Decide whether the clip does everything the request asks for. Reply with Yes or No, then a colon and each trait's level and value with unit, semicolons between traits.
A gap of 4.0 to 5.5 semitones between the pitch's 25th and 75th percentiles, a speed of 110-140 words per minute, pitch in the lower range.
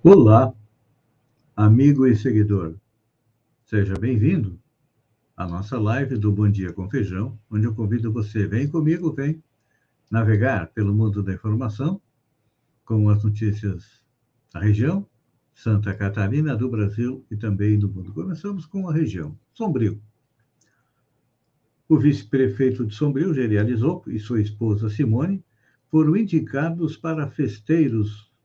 Yes: average, 4.7 semitones; slow, 120 wpm; low, 115 Hz